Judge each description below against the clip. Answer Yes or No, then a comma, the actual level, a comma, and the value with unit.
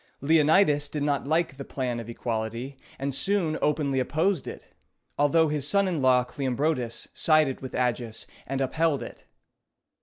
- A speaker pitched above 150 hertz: No, medium, 140 Hz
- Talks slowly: No, average, 150 wpm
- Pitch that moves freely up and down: No, average, 3.5 semitones